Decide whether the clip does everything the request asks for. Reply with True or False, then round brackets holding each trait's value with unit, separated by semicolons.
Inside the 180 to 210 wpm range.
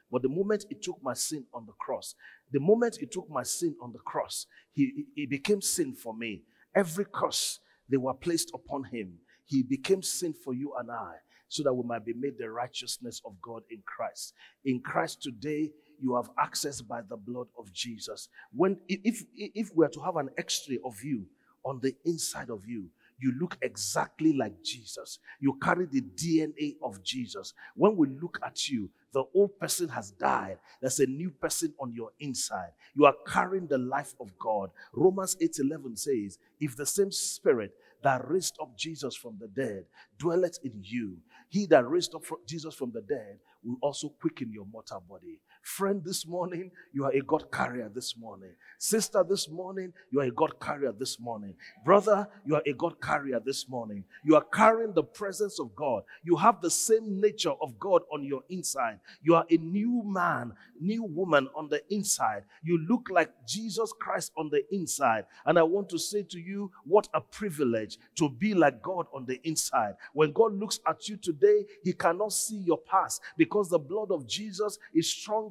True (195 wpm)